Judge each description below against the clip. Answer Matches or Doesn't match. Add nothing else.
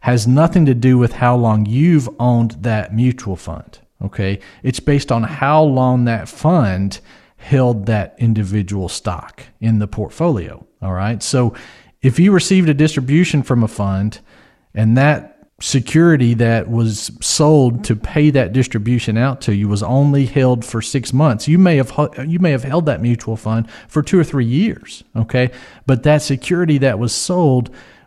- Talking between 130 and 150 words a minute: Doesn't match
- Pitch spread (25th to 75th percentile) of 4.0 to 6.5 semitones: Matches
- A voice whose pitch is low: Matches